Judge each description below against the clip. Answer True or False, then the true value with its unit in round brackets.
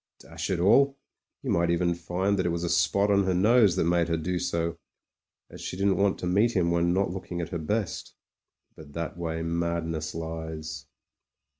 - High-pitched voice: False (85 Hz)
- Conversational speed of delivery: True (195 wpm)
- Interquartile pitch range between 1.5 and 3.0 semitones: True (2.5 semitones)